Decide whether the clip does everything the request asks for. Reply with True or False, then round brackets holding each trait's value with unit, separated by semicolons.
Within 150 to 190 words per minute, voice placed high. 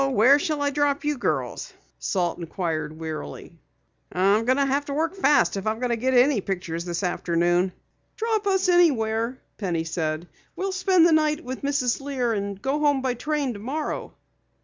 True (160 wpm; 255 Hz)